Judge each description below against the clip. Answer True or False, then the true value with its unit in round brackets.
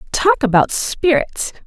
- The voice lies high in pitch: True (285 Hz)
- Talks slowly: True (110 wpm)